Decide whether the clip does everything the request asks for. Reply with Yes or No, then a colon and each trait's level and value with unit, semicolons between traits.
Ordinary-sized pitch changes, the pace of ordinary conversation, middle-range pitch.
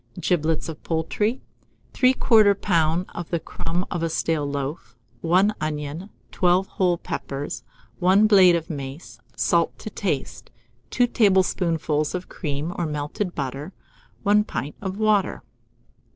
No: average, 4.3 semitones; slow, 130 wpm; medium, 170 Hz